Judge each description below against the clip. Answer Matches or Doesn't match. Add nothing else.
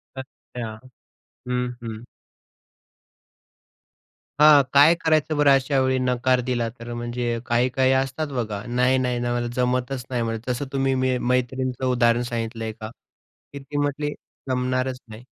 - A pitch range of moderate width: Doesn't match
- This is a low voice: Matches